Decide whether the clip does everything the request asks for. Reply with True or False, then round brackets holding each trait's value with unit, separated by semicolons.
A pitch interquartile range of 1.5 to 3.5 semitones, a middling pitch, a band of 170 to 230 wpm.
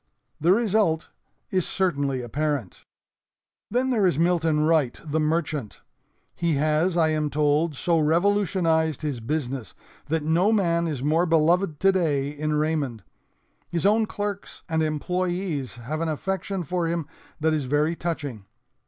False (3.2 semitones; 160 Hz; 140 wpm)